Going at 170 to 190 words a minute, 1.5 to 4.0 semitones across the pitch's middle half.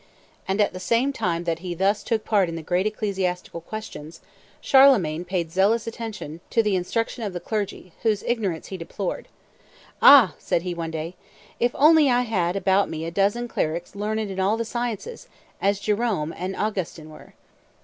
No: average, 180 wpm; average, 4.4 semitones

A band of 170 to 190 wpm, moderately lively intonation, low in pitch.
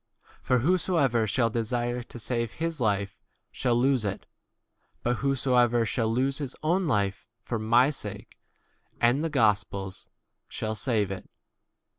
No: average, 155 wpm; average, 3.7 semitones; low, 120 Hz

